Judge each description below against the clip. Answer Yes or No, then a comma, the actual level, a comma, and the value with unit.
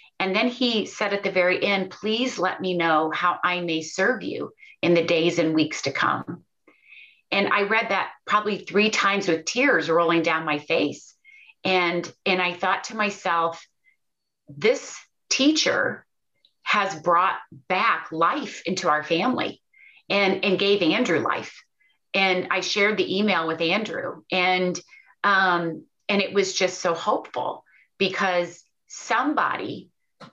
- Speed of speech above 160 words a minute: No, average, 145 wpm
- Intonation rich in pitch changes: No, average, 3.2 semitones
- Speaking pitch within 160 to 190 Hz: Yes, medium, 185 Hz